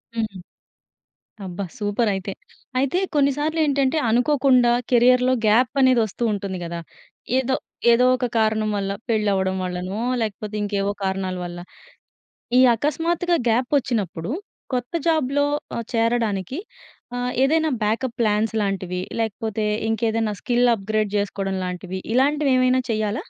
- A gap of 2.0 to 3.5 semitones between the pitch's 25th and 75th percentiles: No, average, 4.3 semitones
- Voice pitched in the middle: No, high, 225 Hz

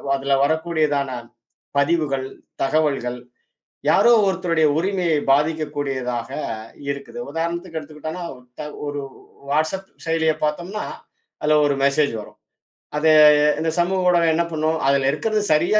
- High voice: No, medium, 155 Hz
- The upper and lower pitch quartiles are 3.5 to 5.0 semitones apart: No, average, 3.0 semitones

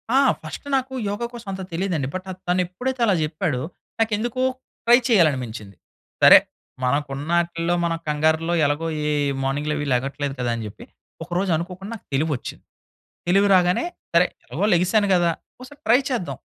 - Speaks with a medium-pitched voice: Yes, medium, 170 Hz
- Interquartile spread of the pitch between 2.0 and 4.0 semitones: No, average, 5.1 semitones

